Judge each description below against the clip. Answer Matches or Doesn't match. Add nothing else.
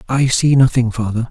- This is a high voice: Doesn't match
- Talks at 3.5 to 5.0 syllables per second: Doesn't match